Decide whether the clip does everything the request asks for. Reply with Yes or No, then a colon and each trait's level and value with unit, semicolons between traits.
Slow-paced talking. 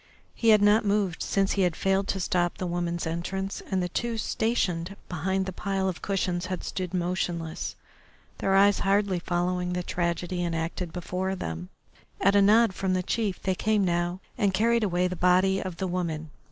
No: average, 185 wpm